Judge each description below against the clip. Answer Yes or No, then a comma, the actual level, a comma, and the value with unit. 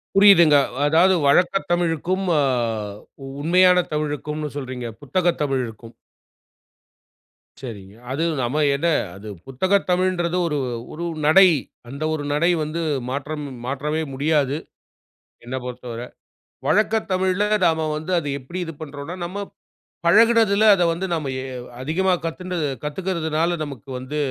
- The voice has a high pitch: No, medium, 155 Hz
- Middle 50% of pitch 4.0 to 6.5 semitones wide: Yes, average, 4.3 semitones